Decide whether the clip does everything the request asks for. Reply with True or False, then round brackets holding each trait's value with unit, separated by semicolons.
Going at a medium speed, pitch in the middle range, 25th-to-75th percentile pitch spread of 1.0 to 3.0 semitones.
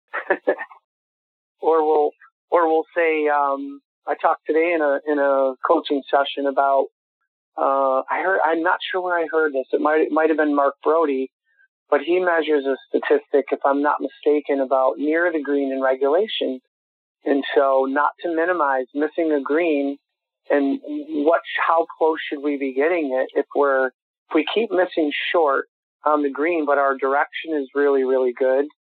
True (175 wpm; 145 Hz; 2.6 semitones)